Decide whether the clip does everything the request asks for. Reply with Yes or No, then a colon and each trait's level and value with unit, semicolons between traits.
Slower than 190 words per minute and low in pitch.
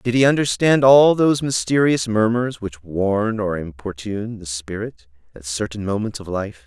Yes: average, 160 wpm; low, 110 Hz